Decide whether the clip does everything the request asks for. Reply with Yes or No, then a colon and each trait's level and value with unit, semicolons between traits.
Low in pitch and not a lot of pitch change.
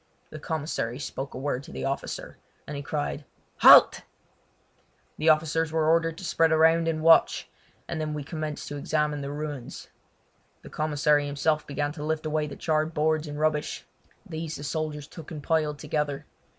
No: medium, 150 Hz; narrow, 1.4 semitones